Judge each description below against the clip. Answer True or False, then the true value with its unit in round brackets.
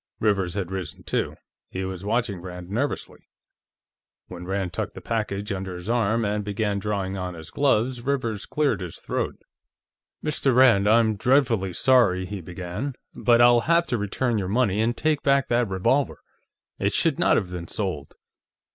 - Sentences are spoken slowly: False (165 wpm)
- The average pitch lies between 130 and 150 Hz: False (105 Hz)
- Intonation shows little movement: False (4.5 semitones)